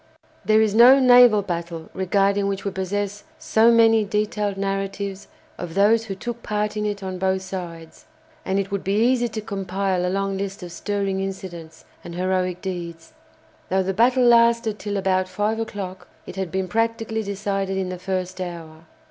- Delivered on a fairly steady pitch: Yes, narrow, 2.3 semitones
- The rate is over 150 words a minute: Yes, average, 175 wpm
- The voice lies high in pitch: Yes, high, 195 Hz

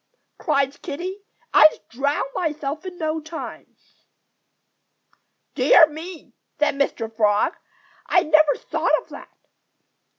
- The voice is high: Yes, very high, 305 Hz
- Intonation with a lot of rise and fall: No, average, 2.7 semitones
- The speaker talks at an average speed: No, slow, 105 wpm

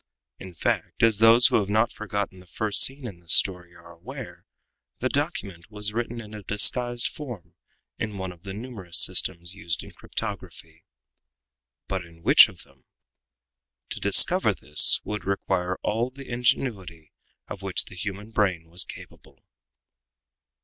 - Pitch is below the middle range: Yes, low, 100 Hz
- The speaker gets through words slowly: No, average, 155 wpm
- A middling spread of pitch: Yes, average, 4.1 semitones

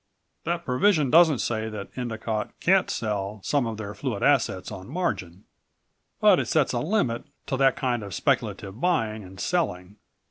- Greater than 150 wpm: Yes, average, 165 wpm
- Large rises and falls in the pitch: Yes, wide, 6.2 semitones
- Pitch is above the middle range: No, low, 115 Hz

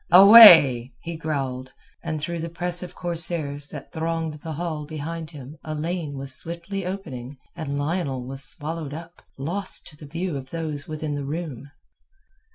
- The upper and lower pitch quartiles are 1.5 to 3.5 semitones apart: Yes, average, 3.1 semitones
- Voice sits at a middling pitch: Yes, medium, 155 Hz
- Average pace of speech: Yes, average, 165 wpm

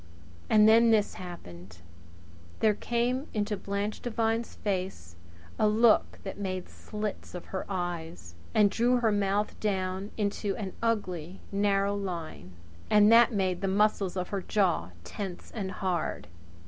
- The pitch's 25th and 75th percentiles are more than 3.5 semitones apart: No, narrow, 2.6 semitones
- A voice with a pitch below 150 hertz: No, high, 200 Hz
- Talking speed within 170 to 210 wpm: No, average, 140 wpm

